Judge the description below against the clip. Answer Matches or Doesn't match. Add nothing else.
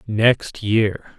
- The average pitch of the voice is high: Doesn't match